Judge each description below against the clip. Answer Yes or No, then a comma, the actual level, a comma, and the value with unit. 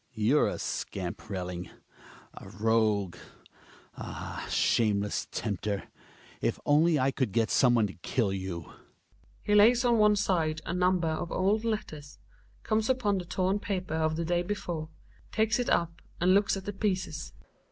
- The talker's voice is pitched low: No, medium, 165 Hz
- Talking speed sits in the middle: Yes, average, 160 wpm